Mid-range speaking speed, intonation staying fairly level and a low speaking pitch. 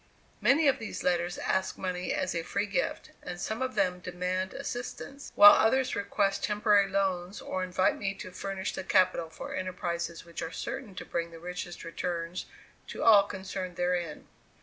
No: average, 170 wpm; narrow, 2.3 semitones; medium, 185 Hz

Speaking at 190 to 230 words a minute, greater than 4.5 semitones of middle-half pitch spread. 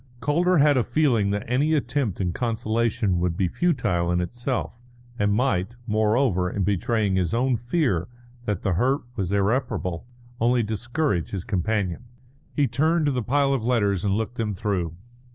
No: average, 165 wpm; average, 4.9 semitones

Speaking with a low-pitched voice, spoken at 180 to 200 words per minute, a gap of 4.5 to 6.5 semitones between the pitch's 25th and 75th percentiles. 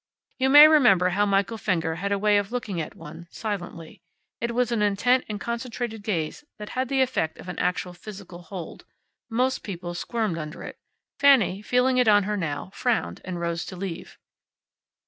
No: high, 205 Hz; average, 185 wpm; average, 5.1 semitones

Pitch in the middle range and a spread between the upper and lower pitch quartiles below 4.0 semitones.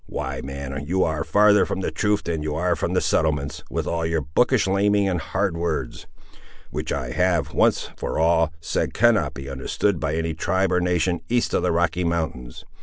No: very low, 85 Hz; average, 3.3 semitones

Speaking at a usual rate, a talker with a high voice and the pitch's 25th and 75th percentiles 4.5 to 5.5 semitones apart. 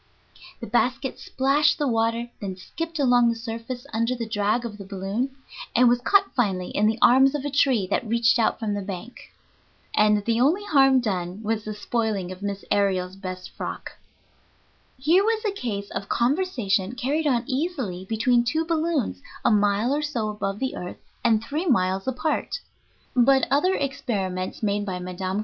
Yes: average, 175 wpm; high, 230 Hz; average, 5.0 semitones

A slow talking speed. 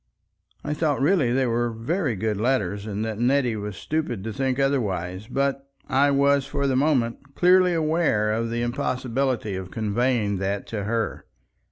No: average, 165 wpm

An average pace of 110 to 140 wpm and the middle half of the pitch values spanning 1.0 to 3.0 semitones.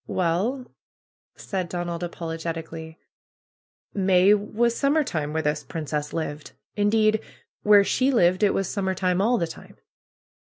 No: slow, 135 wpm; average, 4.3 semitones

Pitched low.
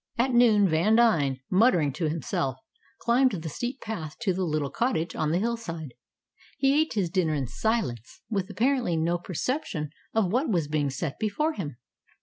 No: medium, 185 Hz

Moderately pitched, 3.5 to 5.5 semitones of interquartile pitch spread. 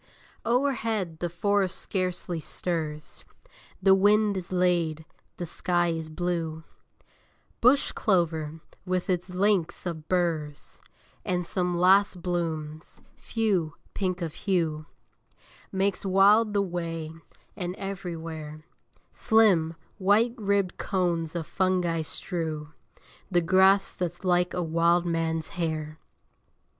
No: medium, 175 Hz; average, 2.8 semitones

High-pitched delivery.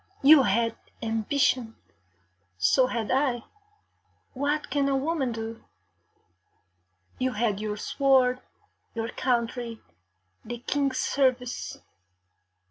Yes: very high, 250 Hz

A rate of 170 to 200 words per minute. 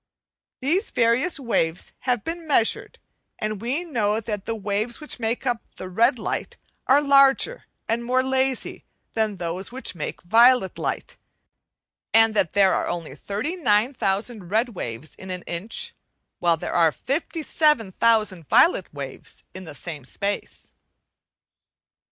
No: average, 145 wpm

